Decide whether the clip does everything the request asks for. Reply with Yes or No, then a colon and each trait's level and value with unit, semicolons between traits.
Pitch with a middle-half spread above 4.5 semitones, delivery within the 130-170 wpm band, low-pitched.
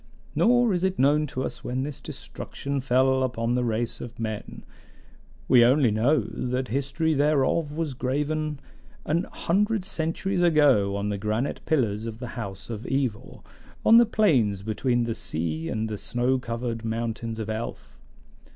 Yes: average, 4.9 semitones; average, 160 wpm; low, 125 Hz